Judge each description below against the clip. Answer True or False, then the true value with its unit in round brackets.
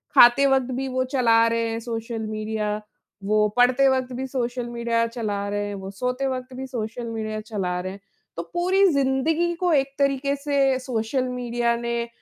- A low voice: False (240 Hz)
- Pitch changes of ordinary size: True (3.2 semitones)